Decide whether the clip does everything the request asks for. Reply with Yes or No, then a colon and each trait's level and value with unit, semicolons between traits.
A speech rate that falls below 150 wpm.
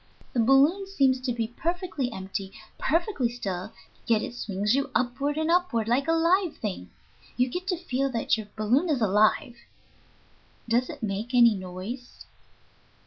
No: average, 155 wpm